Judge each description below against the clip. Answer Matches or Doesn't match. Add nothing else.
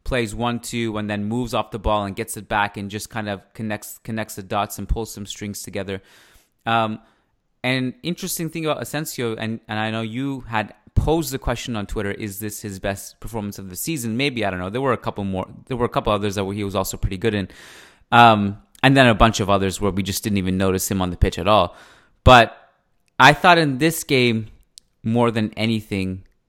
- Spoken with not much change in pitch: Doesn't match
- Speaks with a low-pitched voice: Matches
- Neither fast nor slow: Doesn't match